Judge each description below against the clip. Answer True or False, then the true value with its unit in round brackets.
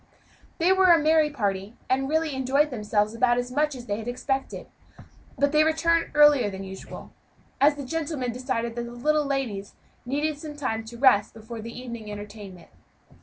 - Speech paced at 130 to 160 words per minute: False (175 wpm)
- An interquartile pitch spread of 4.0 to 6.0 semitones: True (5.0 semitones)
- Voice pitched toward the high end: True (255 Hz)